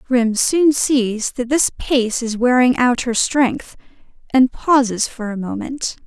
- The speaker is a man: No, female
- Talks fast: No, average, 160 wpm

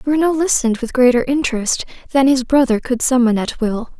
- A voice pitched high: Yes, very high, 255 Hz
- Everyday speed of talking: Yes, average, 180 wpm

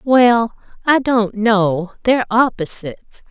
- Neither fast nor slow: No, slow, 110 wpm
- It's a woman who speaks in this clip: Yes, female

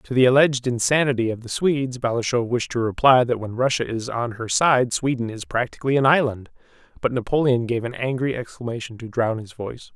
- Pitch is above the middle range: No, low, 125 Hz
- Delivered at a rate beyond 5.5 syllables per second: Yes, 5.8 syllables/s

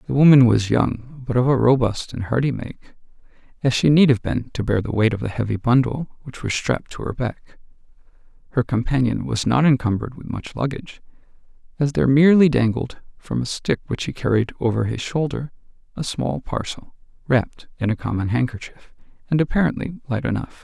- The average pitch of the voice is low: Yes, low, 125 Hz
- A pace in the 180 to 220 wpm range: Yes, average, 185 wpm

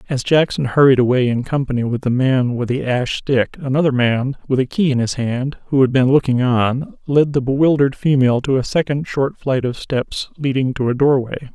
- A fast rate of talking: Yes, fast, 215 wpm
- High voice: No, low, 130 Hz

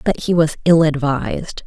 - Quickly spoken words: No, average, 180 wpm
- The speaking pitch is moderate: Yes, medium, 155 Hz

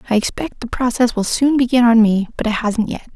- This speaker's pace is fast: Yes, fast, 245 wpm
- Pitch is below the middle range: No, high, 235 Hz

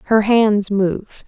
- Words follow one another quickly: No, average, 140 wpm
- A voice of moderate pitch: No, high, 210 Hz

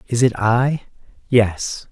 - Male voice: Yes, male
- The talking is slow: Yes, slow, 125 wpm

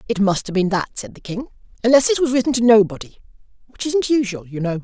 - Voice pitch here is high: Yes, high, 225 Hz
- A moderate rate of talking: No, fast, 235 wpm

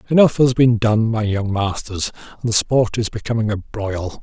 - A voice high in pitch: No, low, 110 Hz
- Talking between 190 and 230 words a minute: Yes, average, 200 wpm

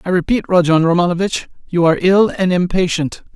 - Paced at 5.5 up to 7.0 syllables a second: Yes, 5.8 syllables/s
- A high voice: No, medium, 180 Hz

